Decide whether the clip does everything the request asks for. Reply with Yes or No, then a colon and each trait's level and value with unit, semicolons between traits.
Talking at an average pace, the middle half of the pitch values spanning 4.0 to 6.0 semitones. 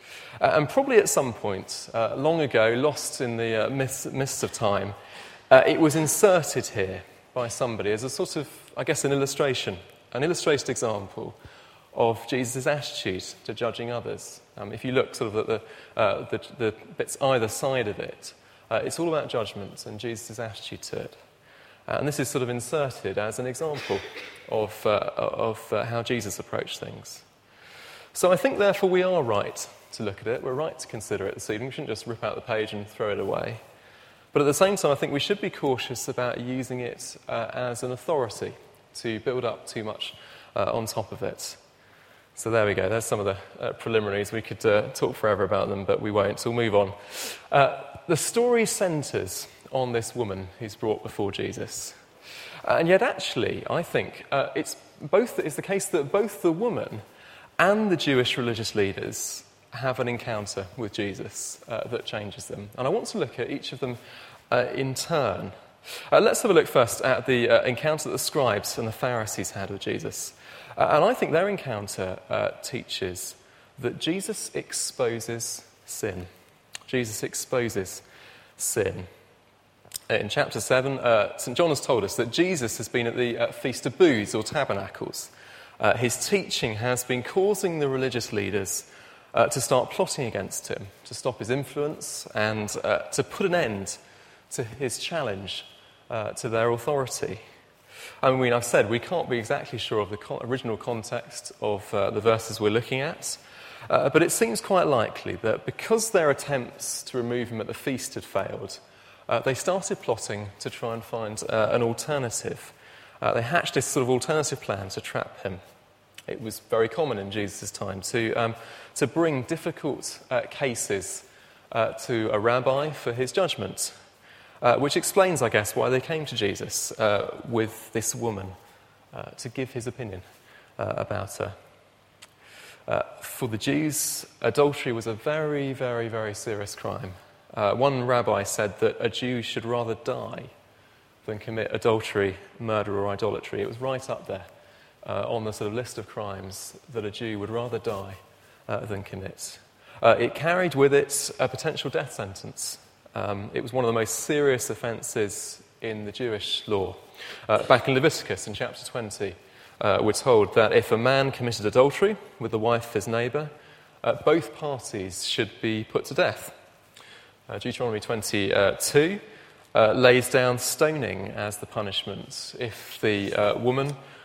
Yes: average, 180 wpm; average, 4.5 semitones